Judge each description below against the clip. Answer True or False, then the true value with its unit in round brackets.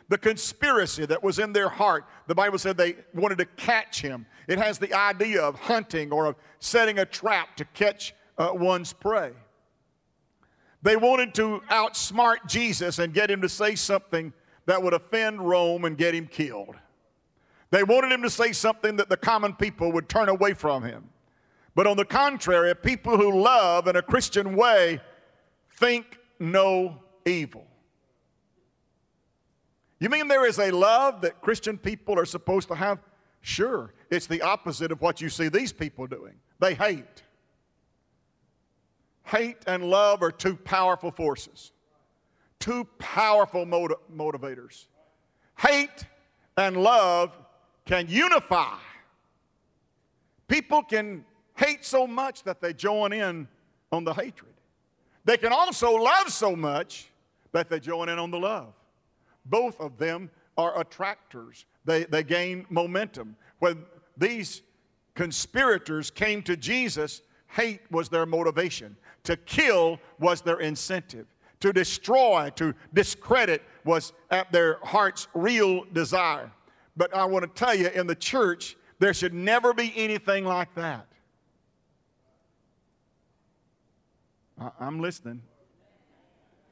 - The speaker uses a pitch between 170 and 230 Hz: True (185 Hz)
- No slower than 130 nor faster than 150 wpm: True (135 wpm)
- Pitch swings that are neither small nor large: True (4.2 semitones)